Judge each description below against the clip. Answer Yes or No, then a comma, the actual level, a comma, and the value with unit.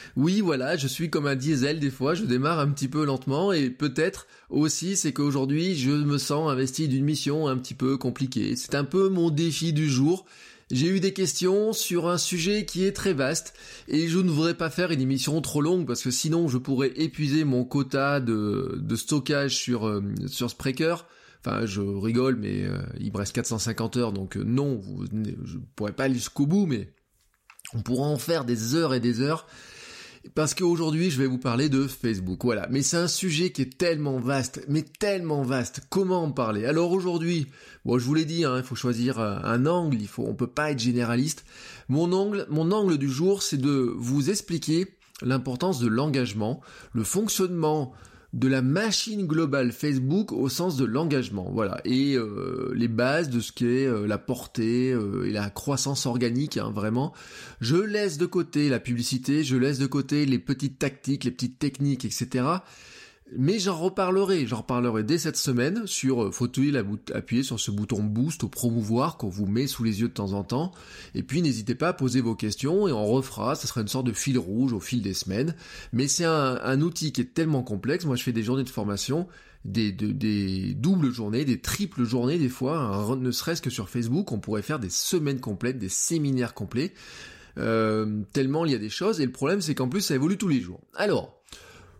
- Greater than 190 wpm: Yes, average, 205 wpm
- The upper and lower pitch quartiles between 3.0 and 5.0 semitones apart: Yes, average, 4.7 semitones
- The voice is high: No, low, 135 Hz